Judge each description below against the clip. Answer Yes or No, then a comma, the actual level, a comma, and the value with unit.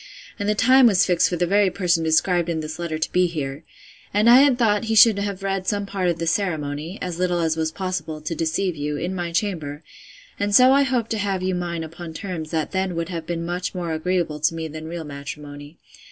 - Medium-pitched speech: Yes, medium, 175 Hz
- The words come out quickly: Yes, fast, 235 wpm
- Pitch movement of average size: Yes, average, 3.7 semitones